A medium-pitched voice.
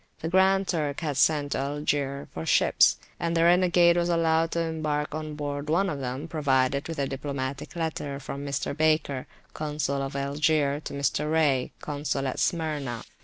Yes: medium, 150 Hz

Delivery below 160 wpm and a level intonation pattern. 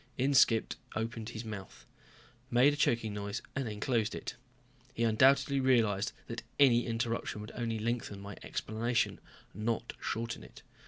Yes: average, 140 wpm; narrow, 2.1 semitones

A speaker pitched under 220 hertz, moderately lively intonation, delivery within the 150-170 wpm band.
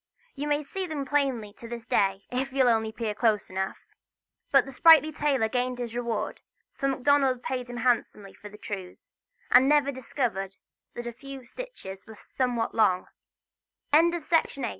No: high, 245 Hz; average, 3.9 semitones; average, 165 wpm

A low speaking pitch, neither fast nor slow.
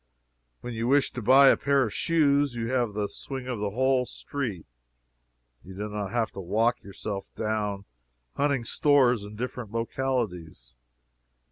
Yes: low, 115 Hz; average, 155 wpm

